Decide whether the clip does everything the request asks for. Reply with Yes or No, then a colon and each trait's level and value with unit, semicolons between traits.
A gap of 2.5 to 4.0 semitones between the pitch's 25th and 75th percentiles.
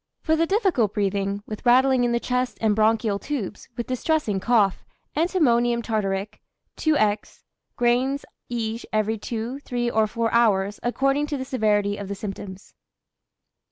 Yes: average, 3.6 semitones